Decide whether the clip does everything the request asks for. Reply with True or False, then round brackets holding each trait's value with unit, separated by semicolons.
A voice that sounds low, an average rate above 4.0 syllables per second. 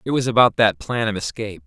True (110 Hz; 6.5 syllables/s)